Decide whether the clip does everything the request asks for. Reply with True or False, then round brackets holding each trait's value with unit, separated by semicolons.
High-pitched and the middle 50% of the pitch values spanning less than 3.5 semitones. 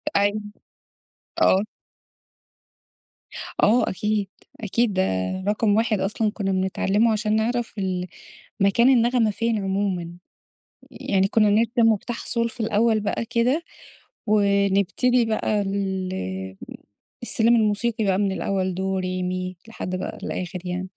True (205 Hz; 3.1 semitones)